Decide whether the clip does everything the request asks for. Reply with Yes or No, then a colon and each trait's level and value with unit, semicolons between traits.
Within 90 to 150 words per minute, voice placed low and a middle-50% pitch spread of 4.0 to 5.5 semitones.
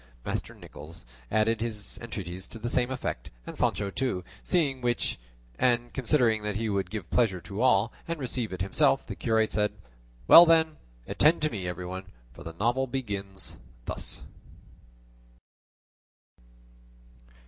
Yes: average, 140 wpm; low, 110 Hz; average, 4.7 semitones